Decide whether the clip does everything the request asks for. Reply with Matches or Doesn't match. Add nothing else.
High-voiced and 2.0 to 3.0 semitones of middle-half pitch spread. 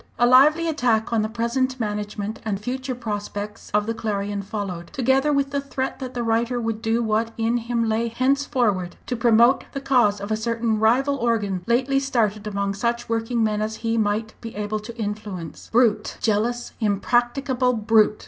Matches